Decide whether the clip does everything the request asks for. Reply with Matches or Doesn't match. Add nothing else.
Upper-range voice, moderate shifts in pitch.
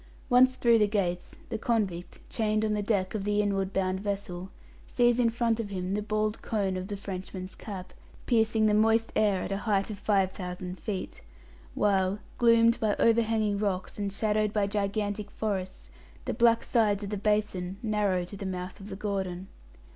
Doesn't match